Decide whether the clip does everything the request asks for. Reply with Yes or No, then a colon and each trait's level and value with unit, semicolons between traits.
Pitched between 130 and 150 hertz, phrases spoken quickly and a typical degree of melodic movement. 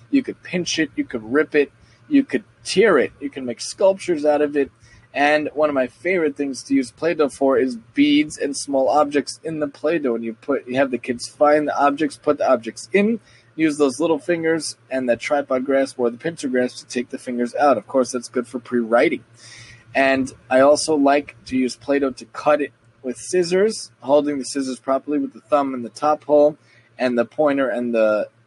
Yes: low, 135 Hz; fast, 215 wpm; average, 3.6 semitones